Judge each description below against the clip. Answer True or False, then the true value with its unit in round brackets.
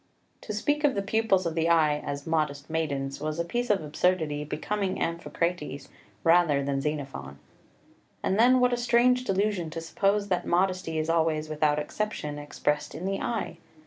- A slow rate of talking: False (170 wpm)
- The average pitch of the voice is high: False (165 Hz)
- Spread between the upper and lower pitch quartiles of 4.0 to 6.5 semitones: True (5.0 semitones)